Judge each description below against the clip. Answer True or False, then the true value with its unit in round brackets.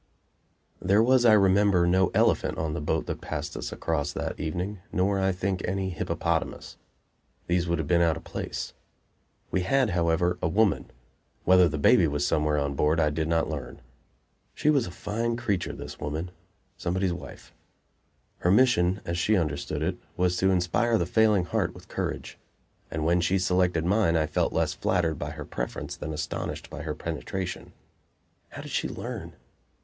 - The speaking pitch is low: True (90 Hz)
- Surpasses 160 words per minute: True (175 wpm)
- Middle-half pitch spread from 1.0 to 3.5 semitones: True (3.2 semitones)